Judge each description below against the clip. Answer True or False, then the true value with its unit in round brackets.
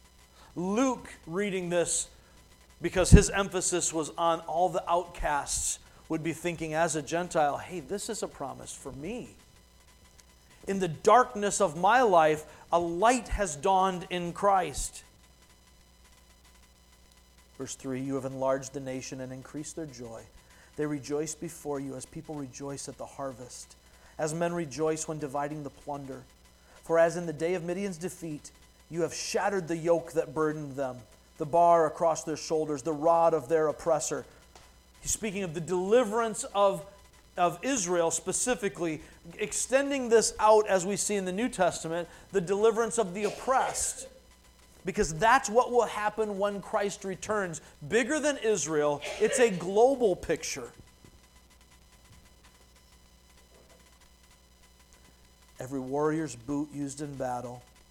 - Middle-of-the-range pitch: True (160 Hz)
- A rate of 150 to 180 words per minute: False (140 wpm)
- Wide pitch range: True (7.1 semitones)